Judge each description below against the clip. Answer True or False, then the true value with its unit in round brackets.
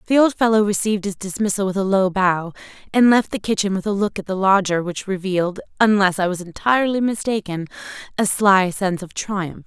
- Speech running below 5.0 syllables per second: True (4.8 syllables/s)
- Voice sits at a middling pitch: False (195 Hz)